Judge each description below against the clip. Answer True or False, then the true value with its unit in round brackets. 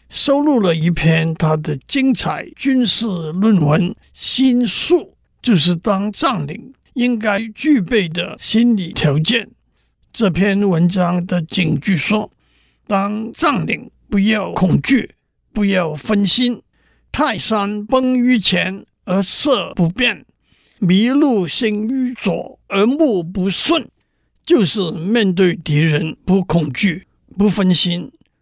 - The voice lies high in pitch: True (200 Hz)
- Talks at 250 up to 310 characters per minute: False (165 characters per minute)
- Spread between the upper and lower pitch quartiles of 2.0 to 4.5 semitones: False (5.1 semitones)